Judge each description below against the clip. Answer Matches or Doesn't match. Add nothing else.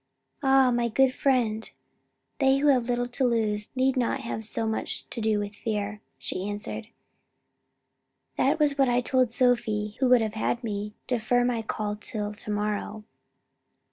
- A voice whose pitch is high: Matches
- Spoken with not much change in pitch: Doesn't match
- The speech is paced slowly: Doesn't match